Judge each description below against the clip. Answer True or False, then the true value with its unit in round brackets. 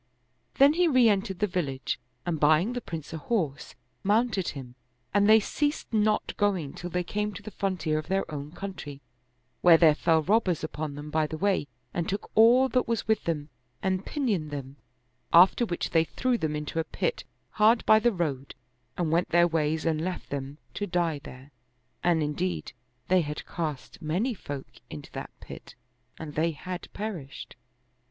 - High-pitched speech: False (175 Hz)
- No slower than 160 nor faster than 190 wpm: True (180 wpm)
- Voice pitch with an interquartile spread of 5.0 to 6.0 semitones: True (5.5 semitones)